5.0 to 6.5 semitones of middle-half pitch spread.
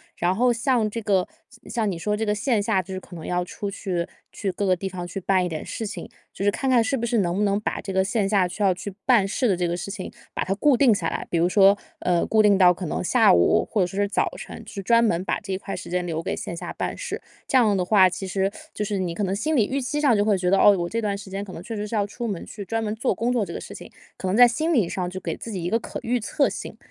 No: average, 3.5 semitones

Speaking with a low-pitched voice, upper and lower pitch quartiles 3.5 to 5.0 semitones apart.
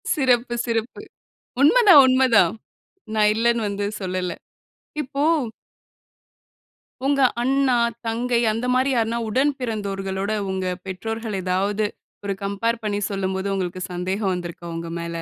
No: high, 215 Hz; average, 4.2 semitones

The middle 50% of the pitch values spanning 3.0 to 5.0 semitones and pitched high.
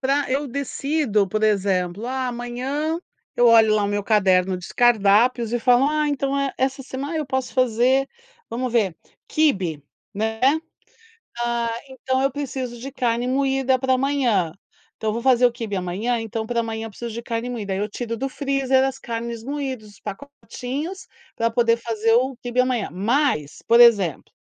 Yes: average, 3.3 semitones; high, 240 Hz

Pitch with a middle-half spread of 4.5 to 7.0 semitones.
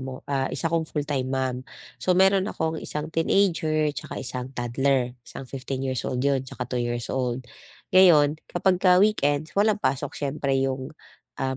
No: average, 3.8 semitones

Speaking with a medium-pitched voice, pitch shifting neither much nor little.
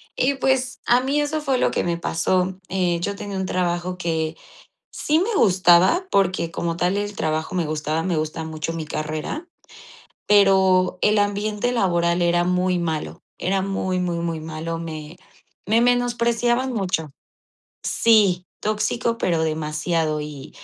Yes: medium, 180 Hz; average, 4.4 semitones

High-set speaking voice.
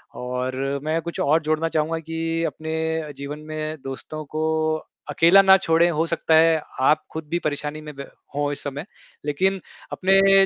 No: medium, 155 Hz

